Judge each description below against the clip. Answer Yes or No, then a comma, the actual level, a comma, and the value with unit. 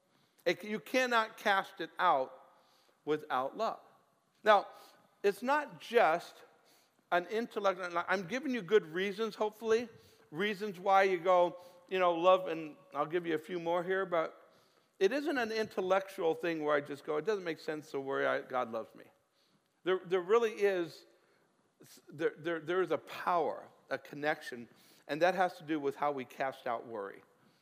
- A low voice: No, medium, 185 Hz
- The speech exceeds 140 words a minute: Yes, average, 170 wpm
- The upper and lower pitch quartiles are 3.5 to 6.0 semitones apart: Yes, average, 4.8 semitones